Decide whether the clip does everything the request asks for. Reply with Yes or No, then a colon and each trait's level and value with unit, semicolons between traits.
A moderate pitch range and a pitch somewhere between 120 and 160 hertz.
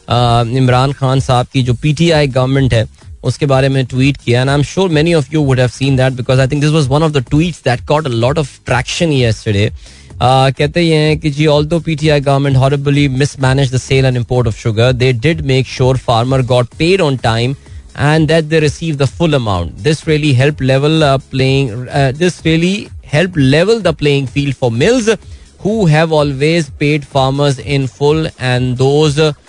Yes: average, 3.2 semitones; medium, 140 Hz